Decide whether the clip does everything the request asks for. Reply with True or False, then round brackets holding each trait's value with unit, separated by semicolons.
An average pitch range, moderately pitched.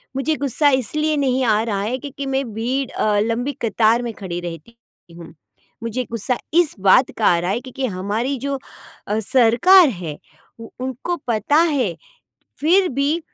False (4.7 semitones; 240 Hz)